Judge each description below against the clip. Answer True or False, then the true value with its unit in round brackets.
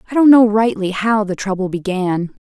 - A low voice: False (205 Hz)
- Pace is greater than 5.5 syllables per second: False (5.1 syllables/s)